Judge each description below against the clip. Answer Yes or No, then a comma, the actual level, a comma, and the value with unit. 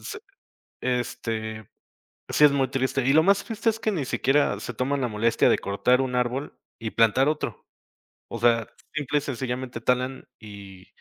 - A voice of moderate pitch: No, low, 125 Hz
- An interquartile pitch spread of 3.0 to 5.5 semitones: Yes, average, 3.5 semitones